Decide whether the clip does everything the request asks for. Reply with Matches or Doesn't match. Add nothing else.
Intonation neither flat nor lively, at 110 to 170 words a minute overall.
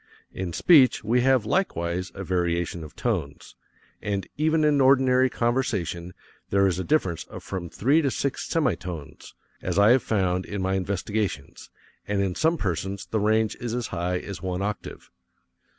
Doesn't match